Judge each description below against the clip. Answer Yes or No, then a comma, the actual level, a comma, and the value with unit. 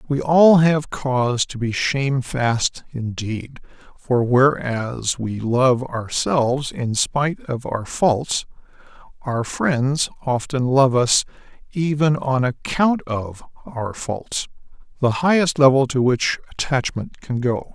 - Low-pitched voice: Yes, low, 130 Hz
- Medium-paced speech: No, slow, 125 wpm